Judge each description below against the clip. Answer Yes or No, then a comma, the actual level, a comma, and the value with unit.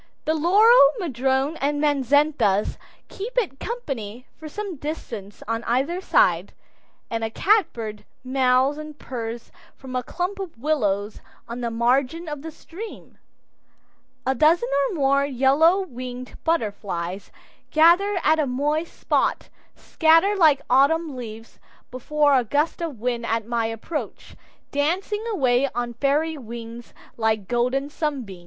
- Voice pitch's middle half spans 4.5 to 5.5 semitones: Yes, average, 5.2 semitones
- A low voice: No, very high, 275 Hz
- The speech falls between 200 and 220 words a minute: No, slow, 135 wpm